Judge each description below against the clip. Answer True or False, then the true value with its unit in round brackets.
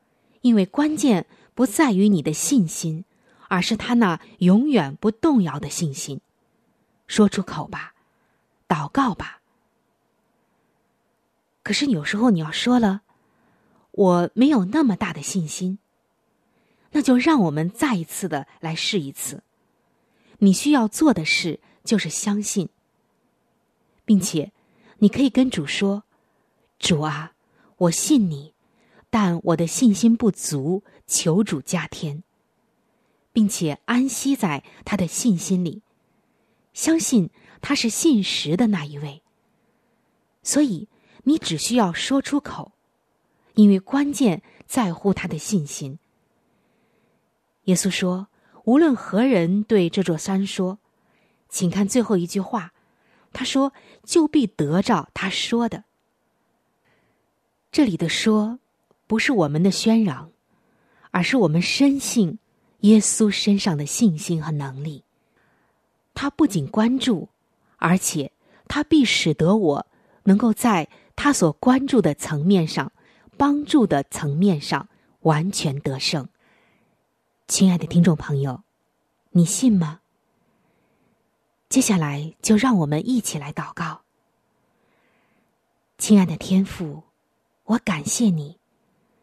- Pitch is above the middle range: True (210 Hz)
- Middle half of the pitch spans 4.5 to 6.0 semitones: True (5.2 semitones)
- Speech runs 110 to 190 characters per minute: True (170 characters per minute)